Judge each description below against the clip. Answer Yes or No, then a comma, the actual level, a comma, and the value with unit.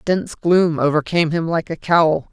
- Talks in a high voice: No, medium, 165 Hz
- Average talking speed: Yes, average, 180 wpm